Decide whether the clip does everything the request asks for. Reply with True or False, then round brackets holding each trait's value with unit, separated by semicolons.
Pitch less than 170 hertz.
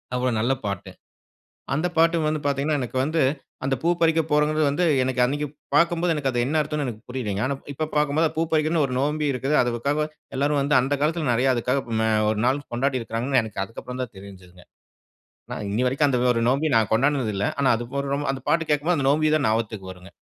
True (140 Hz)